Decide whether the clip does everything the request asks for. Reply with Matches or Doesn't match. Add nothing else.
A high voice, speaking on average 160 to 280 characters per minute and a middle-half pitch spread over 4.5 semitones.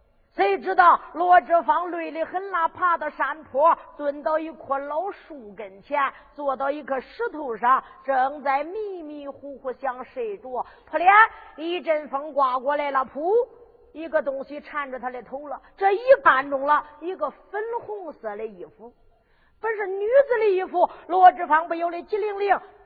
Matches